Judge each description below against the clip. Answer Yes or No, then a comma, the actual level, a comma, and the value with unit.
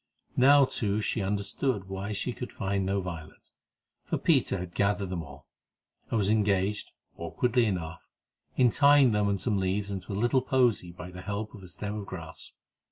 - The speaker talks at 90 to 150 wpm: No, average, 190 wpm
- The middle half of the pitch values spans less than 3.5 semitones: Yes, average, 2.9 semitones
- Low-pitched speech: Yes, low, 100 Hz